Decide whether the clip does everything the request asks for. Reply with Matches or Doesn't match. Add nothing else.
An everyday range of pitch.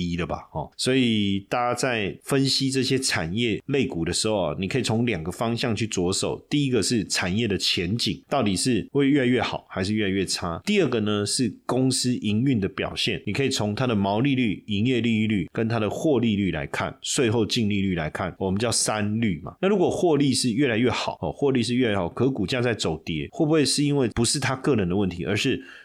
Matches